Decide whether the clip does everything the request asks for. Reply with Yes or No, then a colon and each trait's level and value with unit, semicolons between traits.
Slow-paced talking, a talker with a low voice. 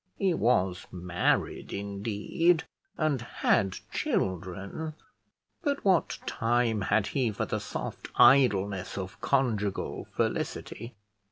Yes: slow, 100 wpm; low, 110 Hz